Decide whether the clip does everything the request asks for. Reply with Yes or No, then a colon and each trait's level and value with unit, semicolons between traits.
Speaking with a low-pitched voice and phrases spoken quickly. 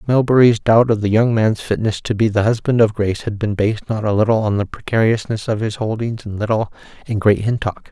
Yes: low, 110 Hz; fast, 230 wpm